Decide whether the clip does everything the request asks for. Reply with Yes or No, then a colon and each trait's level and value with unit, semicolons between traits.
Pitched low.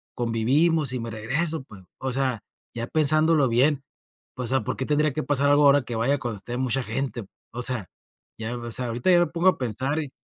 Yes: low, 130 Hz